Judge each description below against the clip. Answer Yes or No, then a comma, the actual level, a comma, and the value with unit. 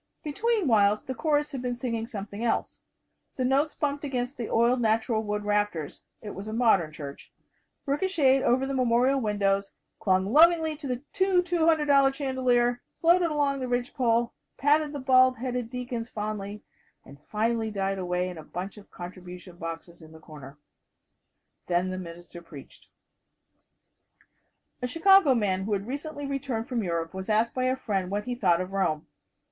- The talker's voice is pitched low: No, high, 235 Hz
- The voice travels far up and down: Yes, wide, 5.7 semitones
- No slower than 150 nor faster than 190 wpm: Yes, average, 165 wpm